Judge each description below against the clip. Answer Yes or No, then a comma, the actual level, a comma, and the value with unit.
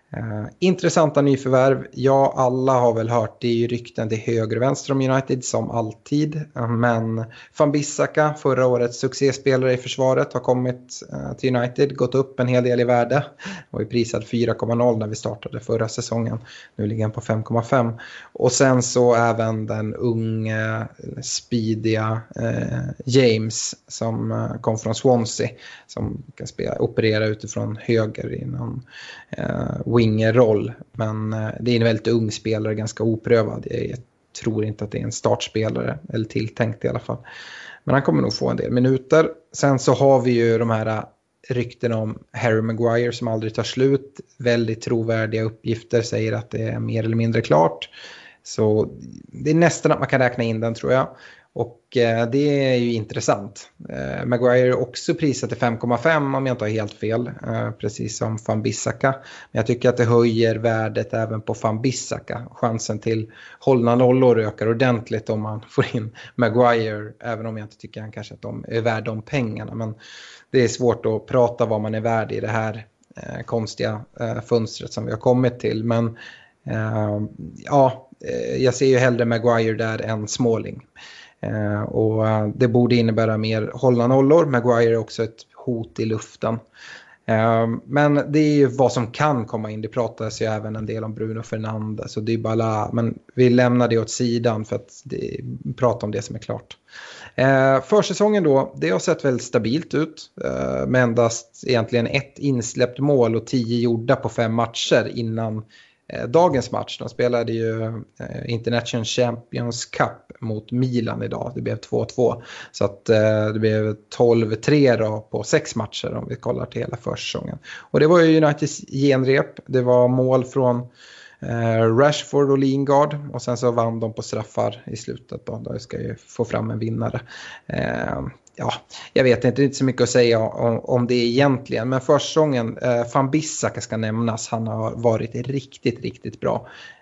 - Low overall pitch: Yes, low, 120 Hz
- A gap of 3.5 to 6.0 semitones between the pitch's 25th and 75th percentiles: No, narrow, 2.5 semitones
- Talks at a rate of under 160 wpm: No, average, 170 wpm